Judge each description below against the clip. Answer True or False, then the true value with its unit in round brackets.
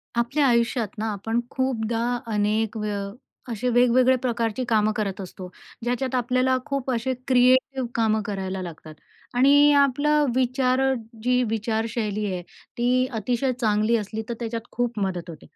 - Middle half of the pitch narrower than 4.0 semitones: True (3.0 semitones)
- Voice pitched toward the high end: True (235 Hz)